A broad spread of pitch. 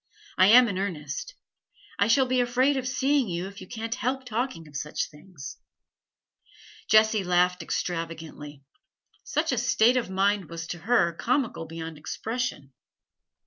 Yes: wide, 7.0 semitones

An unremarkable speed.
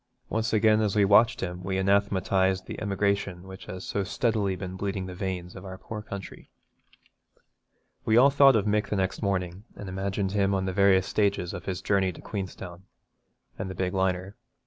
Yes: average, 190 wpm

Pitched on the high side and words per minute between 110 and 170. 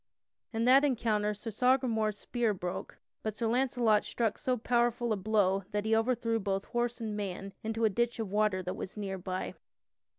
No: high, 220 Hz; average, 185 wpm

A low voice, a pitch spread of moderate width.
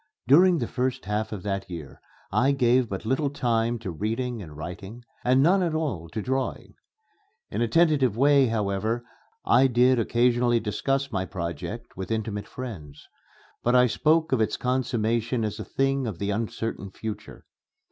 Yes: low, 120 Hz; average, 4.0 semitones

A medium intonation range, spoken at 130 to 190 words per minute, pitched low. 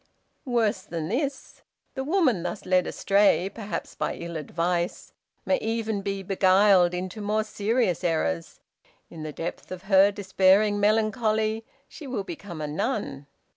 No: average, 3.6 semitones; average, 140 wpm; high, 195 Hz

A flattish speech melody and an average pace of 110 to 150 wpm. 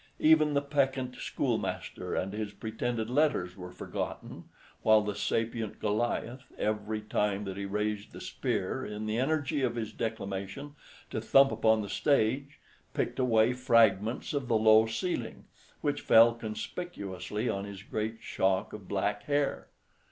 No: average, 3.4 semitones; average, 145 wpm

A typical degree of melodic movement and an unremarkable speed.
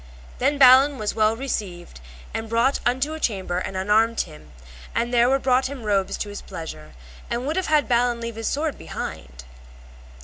Yes: average, 5.0 semitones; average, 190 wpm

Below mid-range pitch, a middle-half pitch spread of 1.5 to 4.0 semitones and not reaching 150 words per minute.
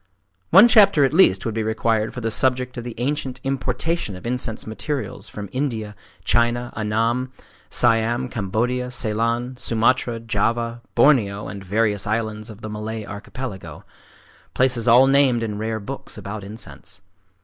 Yes: low, 115 Hz; average, 2.8 semitones; average, 140 wpm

